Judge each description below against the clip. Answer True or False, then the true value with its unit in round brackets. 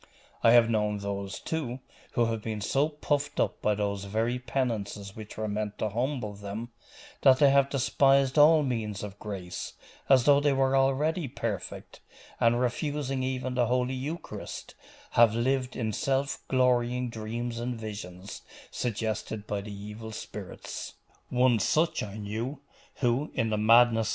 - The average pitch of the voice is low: True (120 Hz)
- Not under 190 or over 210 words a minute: False (155 wpm)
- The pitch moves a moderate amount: True (4.0 semitones)